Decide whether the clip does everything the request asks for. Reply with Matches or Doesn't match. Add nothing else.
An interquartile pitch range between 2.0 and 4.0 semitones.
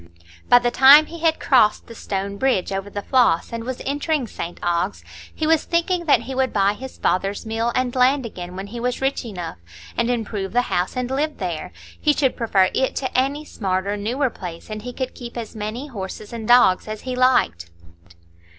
Doesn't match